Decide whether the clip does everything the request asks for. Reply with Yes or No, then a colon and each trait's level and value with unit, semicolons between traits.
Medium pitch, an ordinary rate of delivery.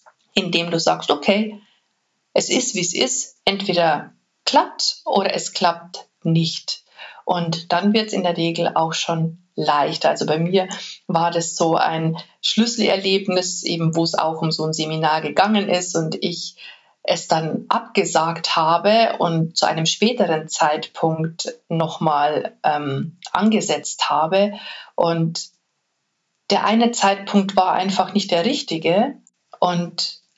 Yes: medium, 170 Hz; average, 135 wpm